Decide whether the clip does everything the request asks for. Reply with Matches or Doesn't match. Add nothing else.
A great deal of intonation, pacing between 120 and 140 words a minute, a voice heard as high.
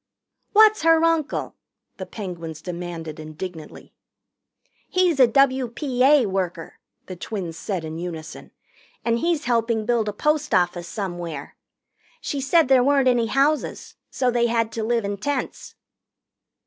Matches